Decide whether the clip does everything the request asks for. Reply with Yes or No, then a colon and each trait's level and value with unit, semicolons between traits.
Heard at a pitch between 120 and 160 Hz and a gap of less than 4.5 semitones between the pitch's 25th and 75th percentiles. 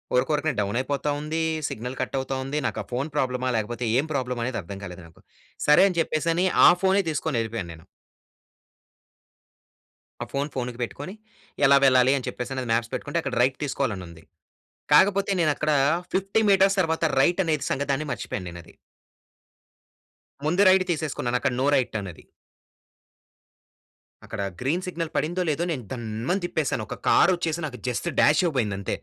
No: low, 135 Hz; average, 5.0 semitones